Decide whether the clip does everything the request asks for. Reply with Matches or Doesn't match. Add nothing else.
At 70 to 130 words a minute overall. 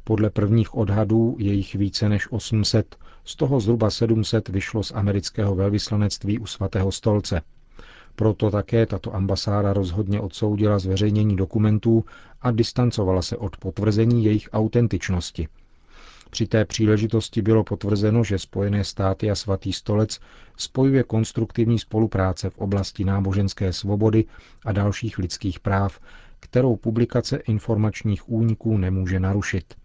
Matches